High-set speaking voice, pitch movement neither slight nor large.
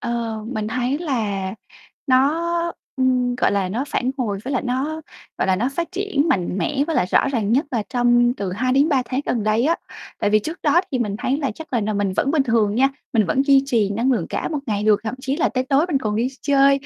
Yes: very high, 250 Hz; average, 4.3 semitones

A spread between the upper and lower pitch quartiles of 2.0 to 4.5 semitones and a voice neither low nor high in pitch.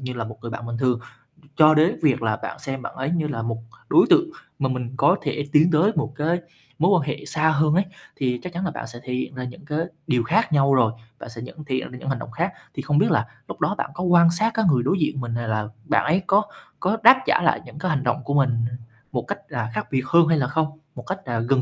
No: average, 5.1 semitones; medium, 145 Hz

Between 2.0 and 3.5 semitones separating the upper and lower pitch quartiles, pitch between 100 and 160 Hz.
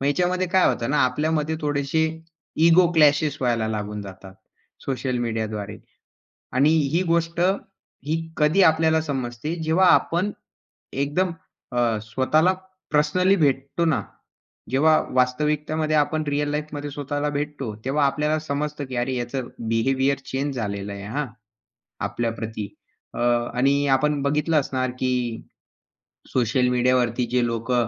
No: average, 4.0 semitones; medium, 140 Hz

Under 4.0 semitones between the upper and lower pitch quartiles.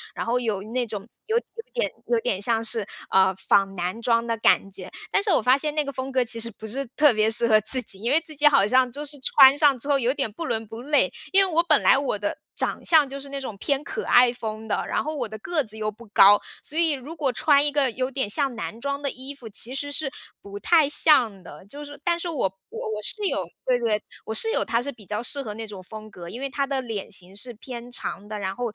No: average, 4.7 semitones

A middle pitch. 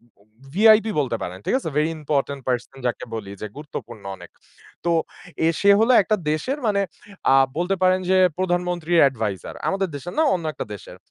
Yes: medium, 160 Hz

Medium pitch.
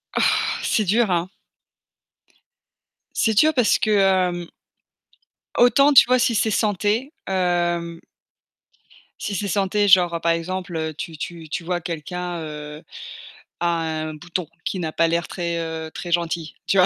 Yes: medium, 175 Hz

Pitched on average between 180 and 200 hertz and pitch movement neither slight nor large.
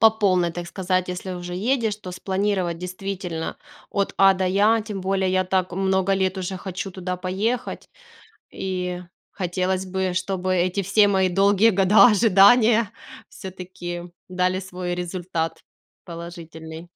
No: medium, 185 Hz; narrow, 1.5 semitones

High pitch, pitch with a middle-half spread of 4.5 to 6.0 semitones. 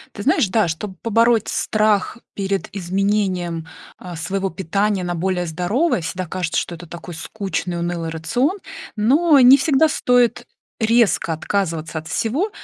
Yes: high, 195 Hz; average, 4.9 semitones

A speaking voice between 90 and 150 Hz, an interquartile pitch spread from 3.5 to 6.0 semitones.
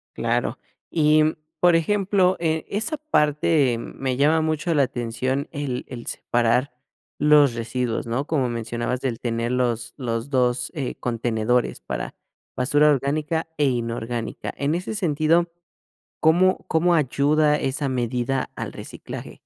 Yes: medium, 140 Hz; average, 4.4 semitones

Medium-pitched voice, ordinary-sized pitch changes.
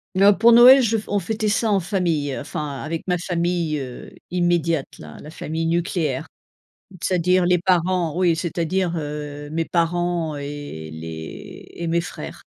Yes: medium, 170 Hz; average, 3.3 semitones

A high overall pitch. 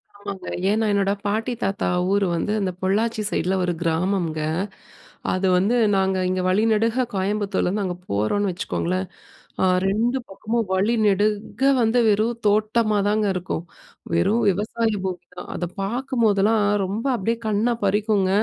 Yes: high, 205 Hz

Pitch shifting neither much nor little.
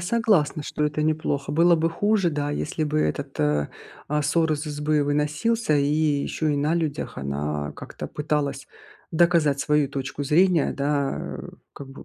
No: narrow, 2.3 semitones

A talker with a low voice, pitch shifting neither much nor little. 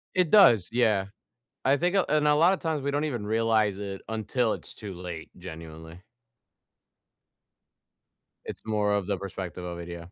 No: low, 105 Hz; wide, 7.7 semitones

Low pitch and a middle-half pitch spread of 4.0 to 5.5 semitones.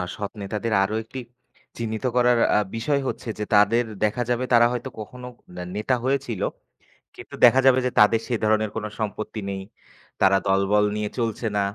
No: low, 110 Hz; average, 2.7 semitones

